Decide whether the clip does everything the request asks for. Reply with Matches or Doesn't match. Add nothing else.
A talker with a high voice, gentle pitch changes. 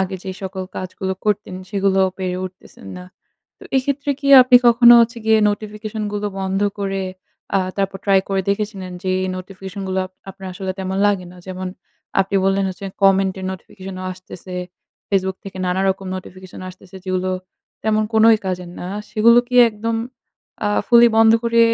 Matches